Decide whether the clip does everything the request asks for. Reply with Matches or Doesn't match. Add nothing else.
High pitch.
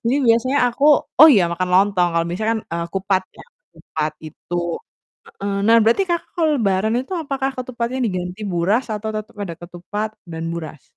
Matches